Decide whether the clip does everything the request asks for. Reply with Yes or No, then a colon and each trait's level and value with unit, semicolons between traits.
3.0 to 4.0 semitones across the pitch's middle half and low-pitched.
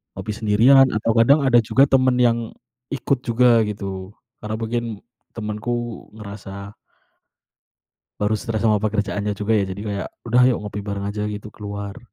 No: narrow, 2.6 semitones; low, 110 Hz